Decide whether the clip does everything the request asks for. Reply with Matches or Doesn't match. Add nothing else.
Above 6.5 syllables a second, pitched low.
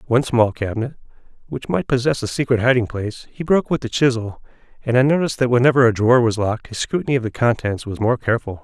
Matches